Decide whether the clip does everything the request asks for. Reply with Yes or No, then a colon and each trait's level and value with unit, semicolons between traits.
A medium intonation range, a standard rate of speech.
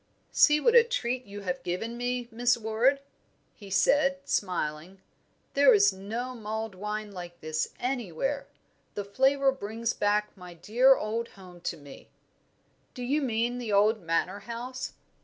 Yes: average, 4.2 semitones; average, 150 wpm